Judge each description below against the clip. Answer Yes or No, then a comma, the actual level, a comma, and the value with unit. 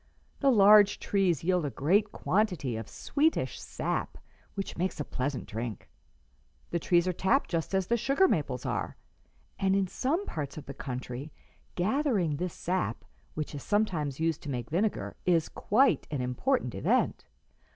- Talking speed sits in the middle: Yes, average, 160 wpm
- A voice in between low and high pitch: Yes, medium, 180 Hz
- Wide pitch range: Yes, wide, 6.2 semitones